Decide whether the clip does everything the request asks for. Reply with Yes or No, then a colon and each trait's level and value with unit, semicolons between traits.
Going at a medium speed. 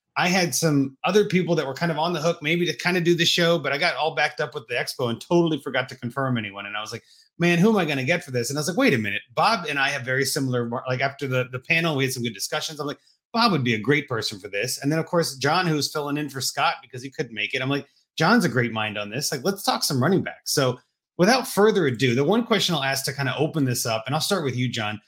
No: fast, 310 wpm